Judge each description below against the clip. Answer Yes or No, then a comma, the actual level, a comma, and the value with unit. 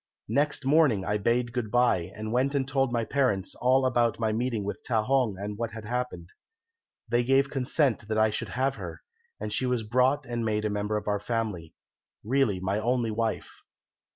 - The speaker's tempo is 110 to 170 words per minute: No, average, 195 wpm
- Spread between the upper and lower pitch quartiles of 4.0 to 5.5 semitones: No, average, 3.3 semitones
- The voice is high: No, low, 115 Hz